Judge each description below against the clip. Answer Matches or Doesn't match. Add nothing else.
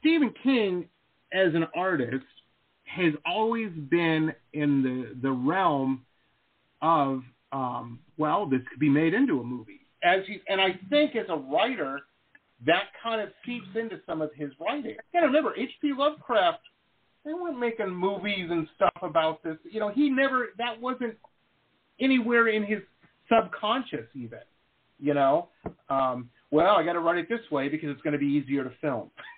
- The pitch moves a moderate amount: Doesn't match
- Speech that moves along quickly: Doesn't match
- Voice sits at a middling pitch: Matches